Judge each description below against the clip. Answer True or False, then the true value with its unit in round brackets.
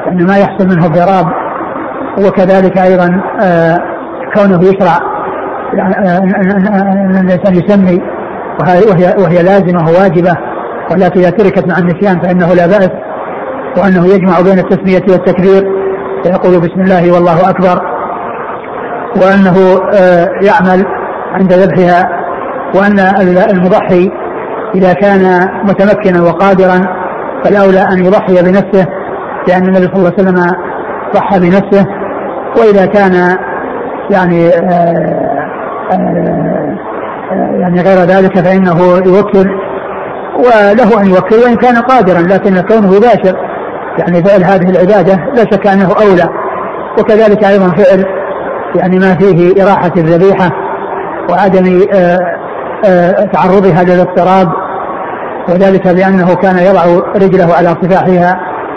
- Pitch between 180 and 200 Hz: True (190 Hz)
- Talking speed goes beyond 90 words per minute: True (100 wpm)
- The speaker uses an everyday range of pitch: False (1.5 semitones)